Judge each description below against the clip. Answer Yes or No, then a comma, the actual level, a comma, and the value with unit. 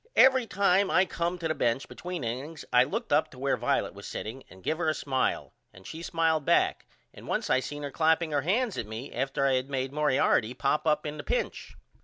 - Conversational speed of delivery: No, fast, 230 wpm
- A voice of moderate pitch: Yes, medium, 150 Hz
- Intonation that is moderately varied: Yes, average, 4.4 semitones